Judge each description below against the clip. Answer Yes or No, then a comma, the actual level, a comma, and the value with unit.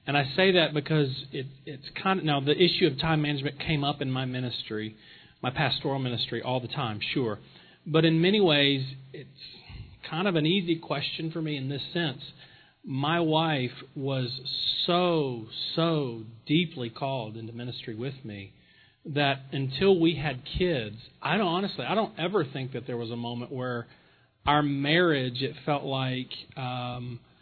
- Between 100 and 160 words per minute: No, average, 170 wpm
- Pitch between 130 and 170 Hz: Yes, medium, 140 Hz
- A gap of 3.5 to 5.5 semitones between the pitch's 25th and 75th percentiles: Yes, average, 4.0 semitones